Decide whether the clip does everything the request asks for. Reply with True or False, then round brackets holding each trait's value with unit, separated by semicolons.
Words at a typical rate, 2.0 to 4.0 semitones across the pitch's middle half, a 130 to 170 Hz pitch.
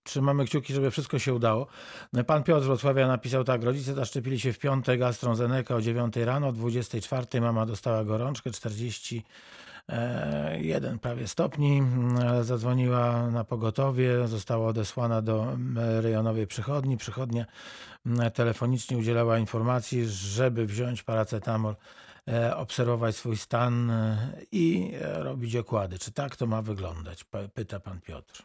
False (120 wpm; 2.4 semitones; 120 Hz)